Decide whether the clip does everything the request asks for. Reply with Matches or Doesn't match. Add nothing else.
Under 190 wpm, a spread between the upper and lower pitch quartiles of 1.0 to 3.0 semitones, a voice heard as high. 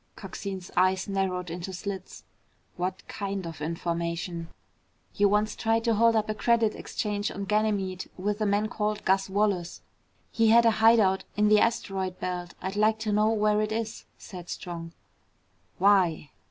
Matches